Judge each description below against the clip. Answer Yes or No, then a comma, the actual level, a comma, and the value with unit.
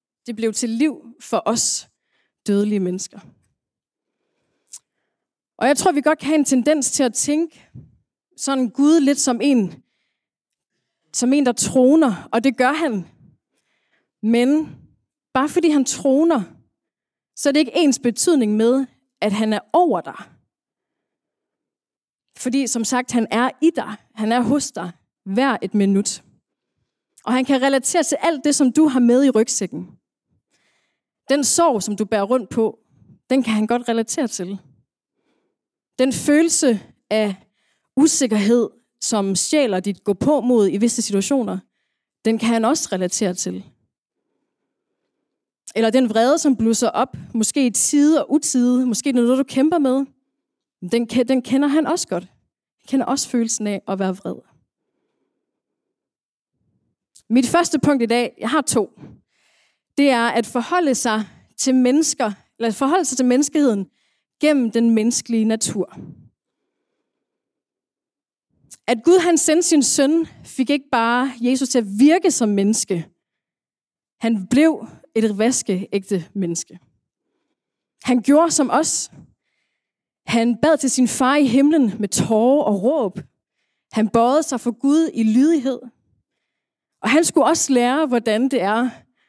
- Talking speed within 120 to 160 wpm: Yes, slow, 145 wpm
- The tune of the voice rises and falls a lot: No, average, 4.4 semitones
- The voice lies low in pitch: No, very high, 250 Hz